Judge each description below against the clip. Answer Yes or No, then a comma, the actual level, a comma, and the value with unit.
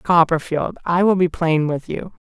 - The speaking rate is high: No, average, 185 wpm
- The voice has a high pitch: No, medium, 170 Hz